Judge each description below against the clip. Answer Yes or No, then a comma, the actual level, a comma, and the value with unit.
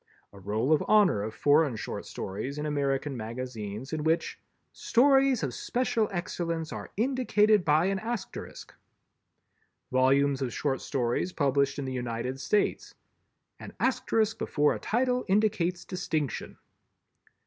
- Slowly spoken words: Yes, slow, 130 wpm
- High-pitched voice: No, medium, 150 Hz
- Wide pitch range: Yes, wide, 7.5 semitones